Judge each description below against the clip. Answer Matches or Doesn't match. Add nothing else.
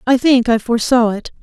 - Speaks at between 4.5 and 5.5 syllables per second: Doesn't match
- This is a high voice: Matches